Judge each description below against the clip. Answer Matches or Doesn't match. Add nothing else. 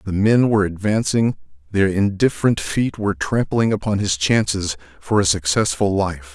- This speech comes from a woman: Doesn't match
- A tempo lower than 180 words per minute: Matches